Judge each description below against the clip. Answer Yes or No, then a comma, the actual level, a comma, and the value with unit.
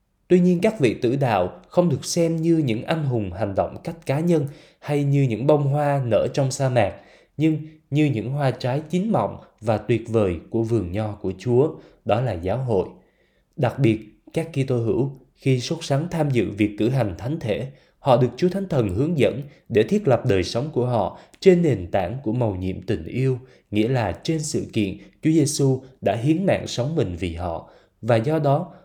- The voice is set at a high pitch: No, low, 130 Hz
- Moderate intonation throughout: No, wide, 5.8 semitones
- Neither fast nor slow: Yes, average, 210 wpm